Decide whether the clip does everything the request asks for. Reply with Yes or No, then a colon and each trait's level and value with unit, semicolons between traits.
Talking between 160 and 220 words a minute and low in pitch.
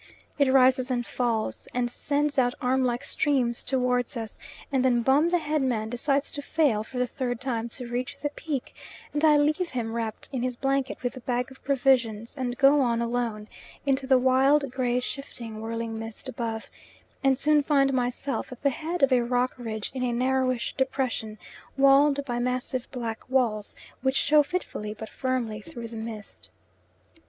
No: average, 180 wpm; very high, 255 Hz